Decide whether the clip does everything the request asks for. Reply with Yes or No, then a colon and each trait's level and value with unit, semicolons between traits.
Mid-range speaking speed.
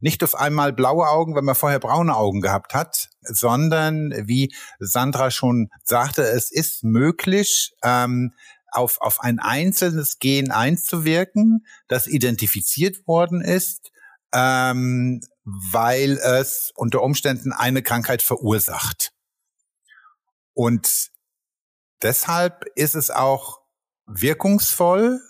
No: slow, 105 wpm